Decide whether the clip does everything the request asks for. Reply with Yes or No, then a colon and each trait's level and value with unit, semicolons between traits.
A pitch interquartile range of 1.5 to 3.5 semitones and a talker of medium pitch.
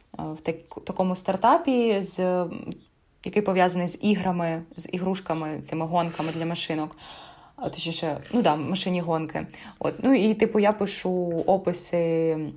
Yes: average, 3.0 semitones; medium, 180 Hz